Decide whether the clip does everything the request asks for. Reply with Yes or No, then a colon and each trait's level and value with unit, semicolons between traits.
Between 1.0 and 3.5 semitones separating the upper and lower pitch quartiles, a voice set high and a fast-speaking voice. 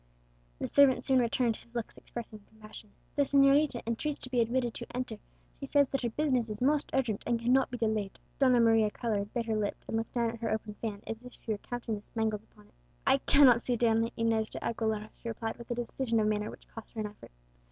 Yes: narrow, 2.4 semitones; high, 230 Hz; fast, 235 wpm